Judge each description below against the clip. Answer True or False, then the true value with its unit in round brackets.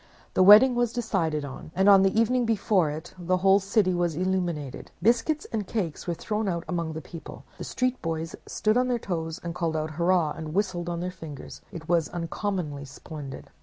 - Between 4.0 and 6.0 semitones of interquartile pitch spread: True (4.3 semitones)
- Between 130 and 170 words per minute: False (190 wpm)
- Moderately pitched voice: True (180 Hz)